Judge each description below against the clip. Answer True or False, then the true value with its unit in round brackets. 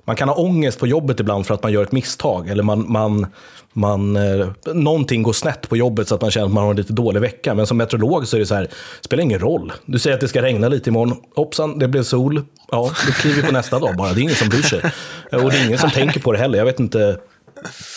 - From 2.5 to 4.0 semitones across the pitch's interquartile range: False (4.5 semitones)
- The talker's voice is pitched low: True (120 Hz)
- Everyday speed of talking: False (280 wpm)